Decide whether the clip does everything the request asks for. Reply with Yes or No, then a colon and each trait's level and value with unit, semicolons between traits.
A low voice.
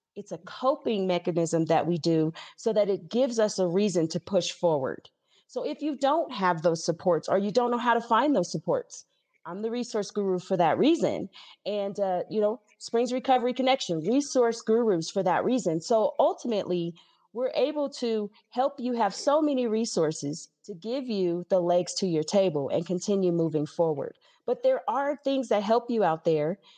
No: high, 205 Hz